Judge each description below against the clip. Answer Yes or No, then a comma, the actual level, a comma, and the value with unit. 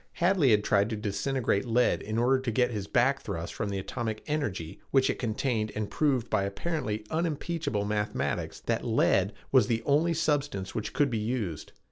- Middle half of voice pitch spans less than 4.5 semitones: No, average, 5.0 semitones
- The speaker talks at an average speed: Yes, average, 180 wpm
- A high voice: No, low, 115 Hz